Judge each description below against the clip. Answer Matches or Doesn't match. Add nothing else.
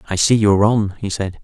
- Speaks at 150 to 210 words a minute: Doesn't match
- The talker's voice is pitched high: Doesn't match